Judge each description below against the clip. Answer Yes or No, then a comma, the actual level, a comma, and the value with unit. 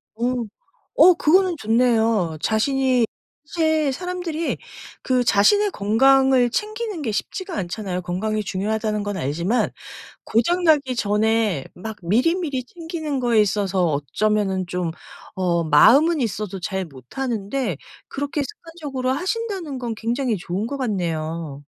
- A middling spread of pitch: No, wide, 6.8 semitones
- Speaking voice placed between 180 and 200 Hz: No, high, 230 Hz